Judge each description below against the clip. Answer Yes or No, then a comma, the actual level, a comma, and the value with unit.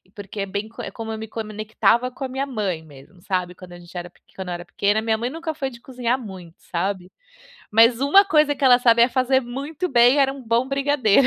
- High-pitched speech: Yes, high, 230 Hz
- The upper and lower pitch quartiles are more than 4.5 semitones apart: Yes, average, 5.2 semitones